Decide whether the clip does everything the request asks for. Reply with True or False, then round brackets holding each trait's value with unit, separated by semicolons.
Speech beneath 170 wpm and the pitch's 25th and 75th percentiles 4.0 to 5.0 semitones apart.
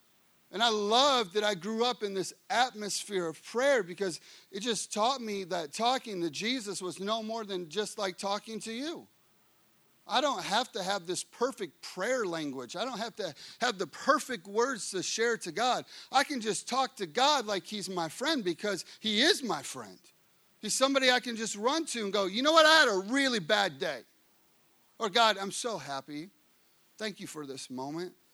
False (200 wpm; 4.4 semitones)